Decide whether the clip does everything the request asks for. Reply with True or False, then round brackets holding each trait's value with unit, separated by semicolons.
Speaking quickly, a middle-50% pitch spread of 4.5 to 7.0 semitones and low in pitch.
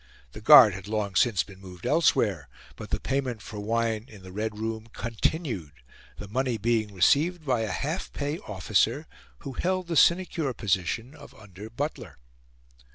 False (160 wpm; 5.5 semitones; 115 Hz)